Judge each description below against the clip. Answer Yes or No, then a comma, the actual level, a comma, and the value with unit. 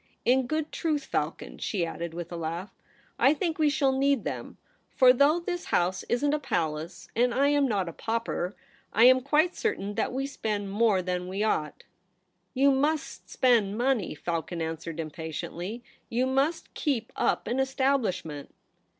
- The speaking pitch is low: No, high, 235 Hz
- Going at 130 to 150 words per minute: No, average, 175 wpm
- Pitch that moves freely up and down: Yes, wide, 7.5 semitones